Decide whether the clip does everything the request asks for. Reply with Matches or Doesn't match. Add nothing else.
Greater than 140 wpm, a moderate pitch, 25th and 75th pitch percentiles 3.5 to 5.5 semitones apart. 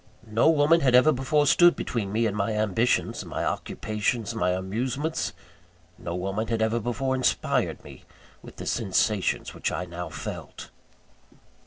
Doesn't match